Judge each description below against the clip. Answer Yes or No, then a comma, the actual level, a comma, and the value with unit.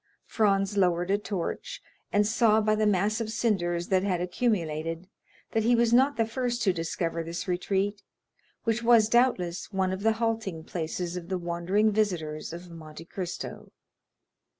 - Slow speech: No, average, 160 wpm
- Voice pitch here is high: Yes, high, 195 Hz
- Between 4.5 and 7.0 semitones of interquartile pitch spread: No, average, 4.1 semitones